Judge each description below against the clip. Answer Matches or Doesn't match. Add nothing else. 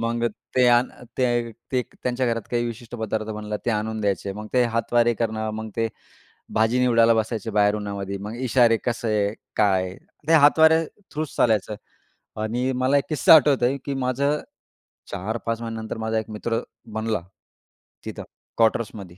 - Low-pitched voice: Matches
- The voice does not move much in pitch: Matches